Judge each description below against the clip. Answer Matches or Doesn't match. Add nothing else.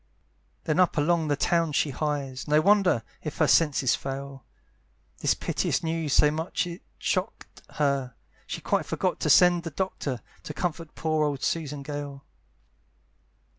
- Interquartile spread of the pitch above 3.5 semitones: Doesn't match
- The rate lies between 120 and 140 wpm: Doesn't match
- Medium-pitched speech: Matches